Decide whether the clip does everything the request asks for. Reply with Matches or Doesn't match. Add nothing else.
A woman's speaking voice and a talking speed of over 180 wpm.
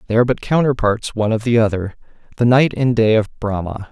Doesn't match